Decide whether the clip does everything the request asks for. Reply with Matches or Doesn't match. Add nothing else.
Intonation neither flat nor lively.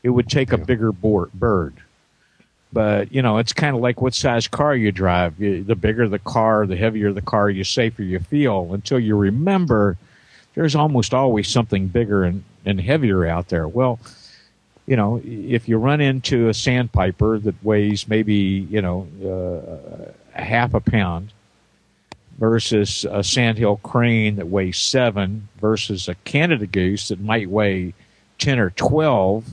Matches